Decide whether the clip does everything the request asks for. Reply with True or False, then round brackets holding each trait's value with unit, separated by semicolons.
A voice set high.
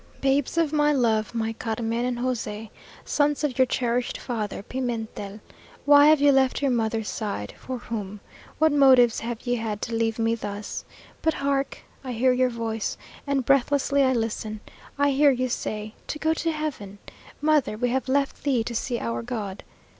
True (245 Hz)